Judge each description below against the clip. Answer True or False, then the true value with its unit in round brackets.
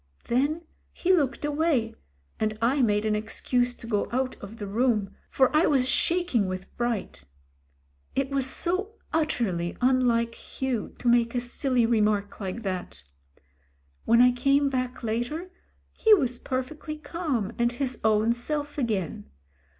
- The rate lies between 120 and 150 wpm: True (145 wpm)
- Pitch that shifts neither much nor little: True (4.1 semitones)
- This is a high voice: True (245 Hz)